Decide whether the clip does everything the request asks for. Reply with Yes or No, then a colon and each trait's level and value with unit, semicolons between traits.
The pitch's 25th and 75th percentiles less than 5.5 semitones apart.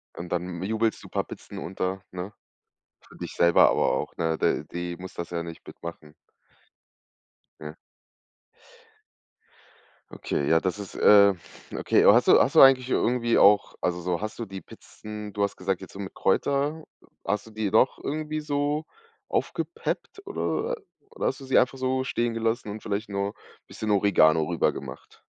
No: wide, 5.8 semitones